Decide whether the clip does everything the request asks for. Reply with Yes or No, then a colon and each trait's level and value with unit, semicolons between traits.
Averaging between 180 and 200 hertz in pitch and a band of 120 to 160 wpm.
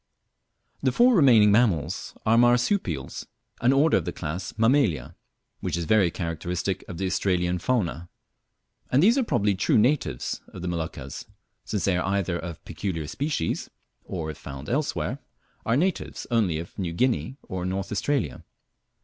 No: very low, 95 Hz; average, 155 wpm